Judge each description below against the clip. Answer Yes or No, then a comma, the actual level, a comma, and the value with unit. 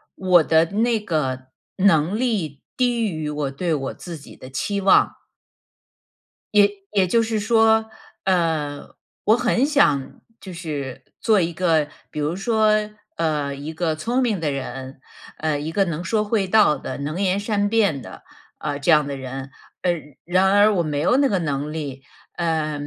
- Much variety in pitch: Yes, wide, 5.8 semitones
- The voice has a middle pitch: Yes, medium, 170 Hz